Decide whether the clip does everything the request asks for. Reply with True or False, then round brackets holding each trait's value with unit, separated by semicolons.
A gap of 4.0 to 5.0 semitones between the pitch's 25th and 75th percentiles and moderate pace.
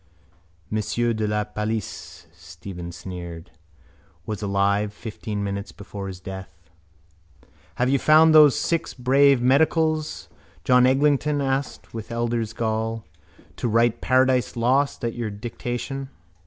False (4.6 semitones; 120 wpm)